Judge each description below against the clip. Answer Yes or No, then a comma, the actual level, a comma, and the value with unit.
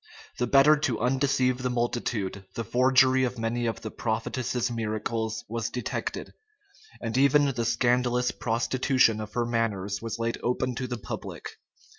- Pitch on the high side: No, low, 120 Hz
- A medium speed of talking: Yes, average, 150 wpm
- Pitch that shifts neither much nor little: No, narrow, 2.1 semitones